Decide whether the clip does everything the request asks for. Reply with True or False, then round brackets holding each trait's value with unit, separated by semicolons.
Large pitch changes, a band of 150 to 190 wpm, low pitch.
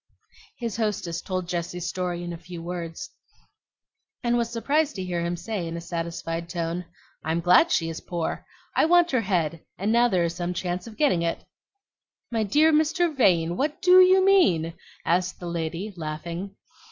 False (5.7 semitones; 175 wpm; 180 Hz)